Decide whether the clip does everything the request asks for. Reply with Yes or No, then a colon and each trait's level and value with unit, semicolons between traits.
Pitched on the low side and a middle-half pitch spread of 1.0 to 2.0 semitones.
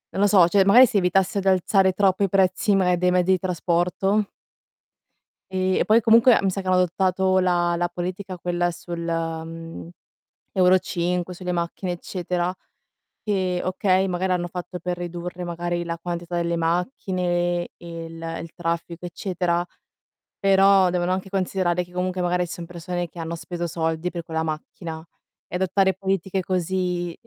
No: medium, 180 Hz; narrow, 1.6 semitones